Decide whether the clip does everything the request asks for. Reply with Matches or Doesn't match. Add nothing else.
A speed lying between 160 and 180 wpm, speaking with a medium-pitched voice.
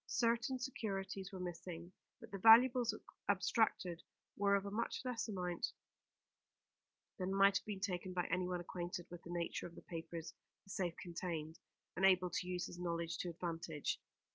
Matches